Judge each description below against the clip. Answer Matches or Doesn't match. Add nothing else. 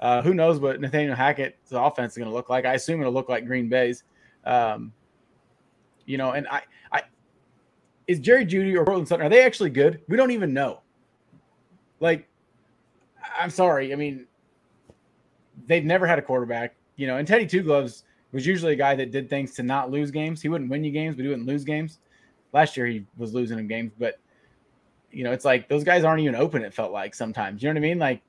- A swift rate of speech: Matches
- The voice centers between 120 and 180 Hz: Matches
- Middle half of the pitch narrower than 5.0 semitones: Matches